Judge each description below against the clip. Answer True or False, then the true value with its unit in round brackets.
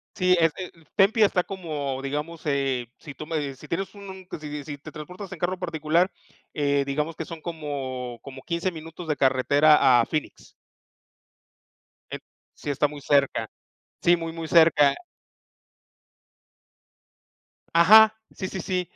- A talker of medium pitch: True (155 Hz)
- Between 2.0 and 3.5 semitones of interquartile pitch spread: False (3.9 semitones)